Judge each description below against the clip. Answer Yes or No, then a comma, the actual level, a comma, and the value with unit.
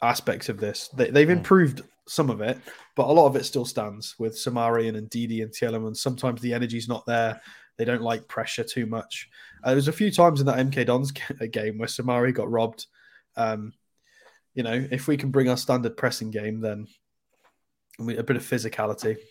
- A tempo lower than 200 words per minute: No, fast, 205 wpm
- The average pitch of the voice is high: No, low, 120 Hz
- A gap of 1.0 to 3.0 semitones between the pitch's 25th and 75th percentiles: Yes, narrow, 2.6 semitones